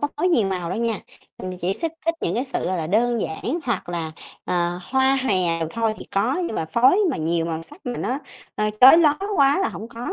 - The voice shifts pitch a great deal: Yes, wide, 7.0 semitones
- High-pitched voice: Yes, high, 225 Hz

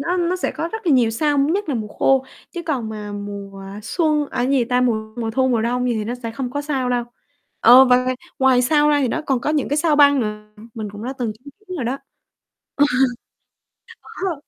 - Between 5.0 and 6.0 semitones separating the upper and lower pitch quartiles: No, average, 4.4 semitones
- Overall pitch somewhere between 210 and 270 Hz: Yes, very high, 255 Hz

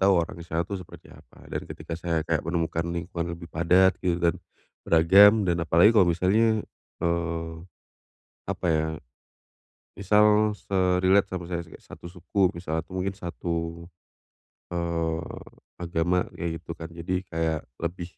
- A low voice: Yes, very low, 85 Hz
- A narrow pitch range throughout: Yes, narrow, 2.0 semitones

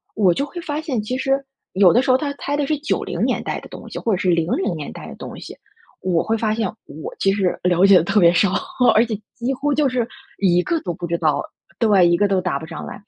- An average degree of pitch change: No, wide, 6.5 semitones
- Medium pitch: No, high, 205 Hz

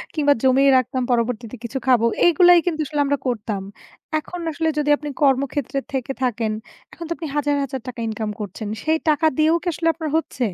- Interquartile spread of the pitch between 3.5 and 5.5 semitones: Yes, average, 4.3 semitones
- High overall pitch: Yes, very high, 275 Hz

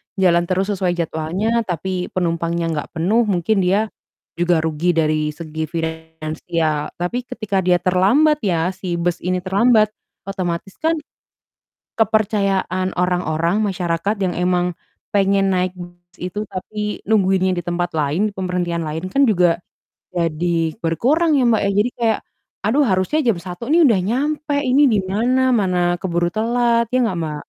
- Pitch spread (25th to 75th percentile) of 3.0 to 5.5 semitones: Yes, average, 3.8 semitones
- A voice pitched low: No, medium, 185 Hz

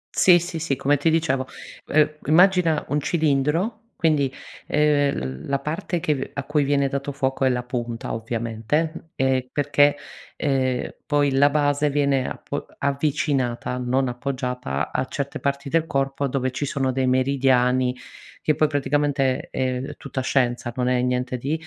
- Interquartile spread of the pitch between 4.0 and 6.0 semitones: No, narrow, 2.5 semitones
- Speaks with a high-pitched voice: No, medium, 140 Hz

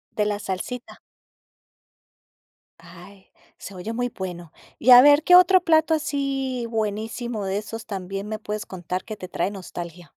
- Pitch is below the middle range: No, high, 215 Hz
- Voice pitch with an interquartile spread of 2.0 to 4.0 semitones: No, average, 4.9 semitones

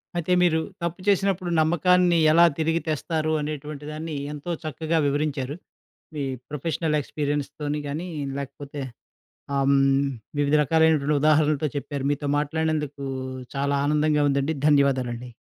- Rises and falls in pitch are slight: Yes, narrow, 2.2 semitones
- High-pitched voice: No, medium, 150 Hz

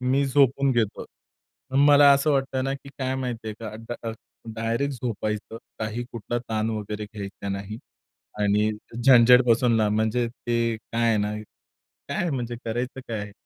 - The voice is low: Yes, low, 115 Hz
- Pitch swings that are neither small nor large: Yes, average, 3.2 semitones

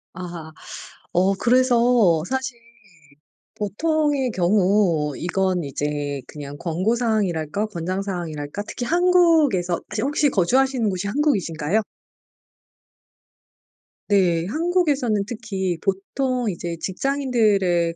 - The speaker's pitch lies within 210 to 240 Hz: No, high, 200 Hz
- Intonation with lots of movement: Yes, wide, 6.7 semitones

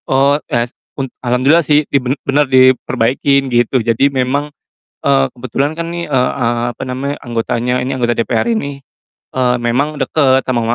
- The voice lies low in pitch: Yes, low, 130 Hz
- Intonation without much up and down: Yes, narrow, 2.3 semitones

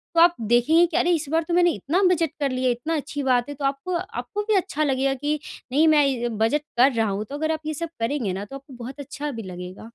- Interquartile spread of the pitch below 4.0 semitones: No, average, 4.6 semitones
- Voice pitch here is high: Yes, very high, 280 Hz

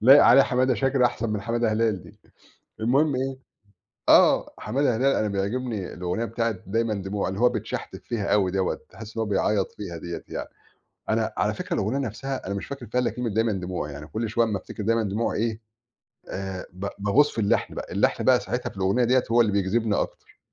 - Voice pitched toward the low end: Yes, low, 110 Hz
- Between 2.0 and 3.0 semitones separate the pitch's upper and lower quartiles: No, average, 3.6 semitones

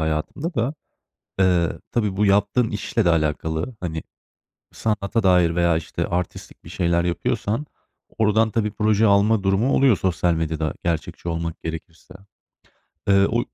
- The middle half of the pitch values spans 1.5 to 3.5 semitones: No, average, 4.5 semitones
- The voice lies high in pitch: No, very low, 95 Hz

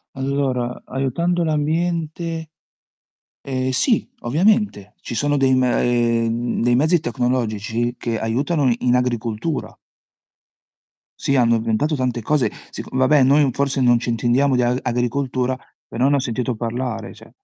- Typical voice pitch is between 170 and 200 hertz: No, low, 130 Hz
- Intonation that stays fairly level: No, average, 3.1 semitones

